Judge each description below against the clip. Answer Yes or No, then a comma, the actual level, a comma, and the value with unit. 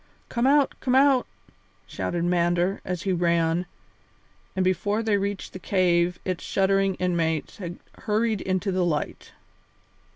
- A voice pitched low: No, medium, 185 Hz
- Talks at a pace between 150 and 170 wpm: No, slow, 135 wpm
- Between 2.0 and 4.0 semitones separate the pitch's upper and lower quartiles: Yes, average, 2.8 semitones